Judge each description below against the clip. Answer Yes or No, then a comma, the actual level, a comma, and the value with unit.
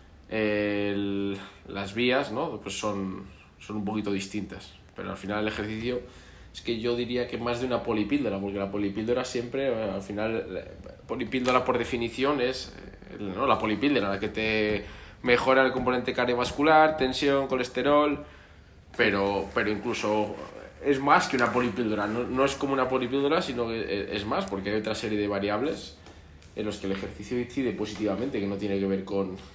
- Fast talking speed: No, average, 170 wpm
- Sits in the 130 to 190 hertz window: No, low, 105 Hz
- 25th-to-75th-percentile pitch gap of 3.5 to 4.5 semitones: Yes, average, 3.9 semitones